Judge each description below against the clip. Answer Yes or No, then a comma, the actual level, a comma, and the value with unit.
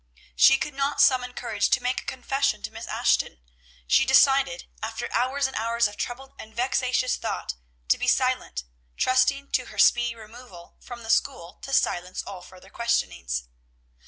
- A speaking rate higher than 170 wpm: No, average, 165 wpm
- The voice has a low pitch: No, high, 245 Hz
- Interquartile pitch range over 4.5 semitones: No, average, 3.4 semitones